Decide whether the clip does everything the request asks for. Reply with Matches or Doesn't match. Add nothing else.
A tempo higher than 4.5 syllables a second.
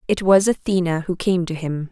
Matches